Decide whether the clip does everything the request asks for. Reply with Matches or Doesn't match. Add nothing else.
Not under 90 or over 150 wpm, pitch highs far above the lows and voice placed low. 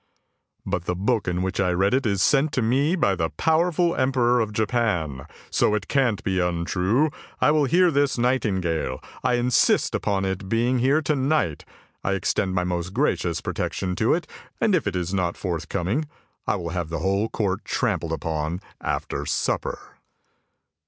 Doesn't match